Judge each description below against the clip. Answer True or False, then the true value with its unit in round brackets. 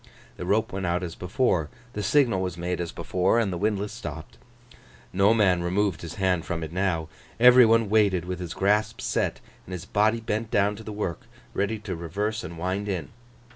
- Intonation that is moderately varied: True (3.3 semitones)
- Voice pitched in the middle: False (95 Hz)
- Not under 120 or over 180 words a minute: False (200 wpm)